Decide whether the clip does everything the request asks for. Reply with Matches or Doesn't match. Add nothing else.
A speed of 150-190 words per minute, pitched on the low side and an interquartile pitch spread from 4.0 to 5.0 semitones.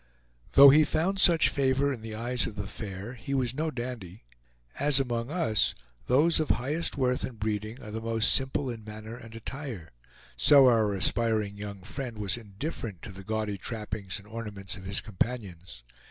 Matches